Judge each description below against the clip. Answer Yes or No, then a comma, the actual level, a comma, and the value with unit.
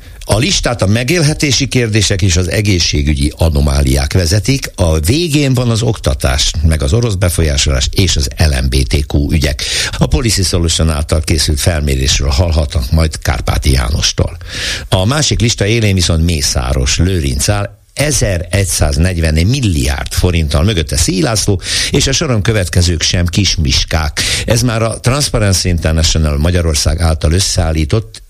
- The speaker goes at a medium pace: Yes, average, 125 wpm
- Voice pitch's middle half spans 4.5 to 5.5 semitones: Yes, average, 4.9 semitones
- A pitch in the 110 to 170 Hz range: No, very low, 90 Hz